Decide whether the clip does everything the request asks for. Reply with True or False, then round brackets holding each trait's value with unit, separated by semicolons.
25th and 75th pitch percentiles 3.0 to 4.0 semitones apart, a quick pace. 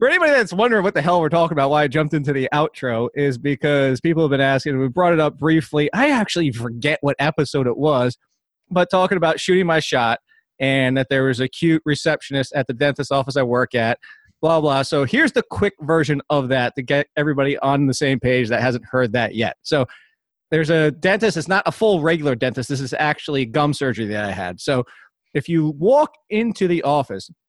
True (3.6 semitones; 220 wpm)